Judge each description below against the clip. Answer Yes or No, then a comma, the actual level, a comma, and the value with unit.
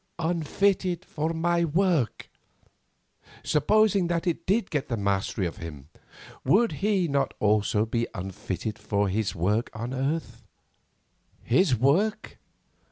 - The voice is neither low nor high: Yes, medium, 145 Hz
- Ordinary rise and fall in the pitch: No, wide, 8.7 semitones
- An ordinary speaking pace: No, slow, 120 wpm